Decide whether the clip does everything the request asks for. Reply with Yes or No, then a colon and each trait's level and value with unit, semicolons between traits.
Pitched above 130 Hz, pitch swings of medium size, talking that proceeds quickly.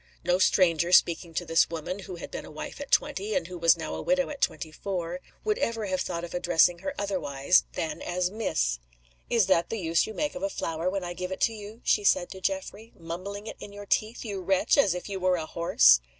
Yes: medium, 185 Hz; average, 3.4 semitones; fast, 240 wpm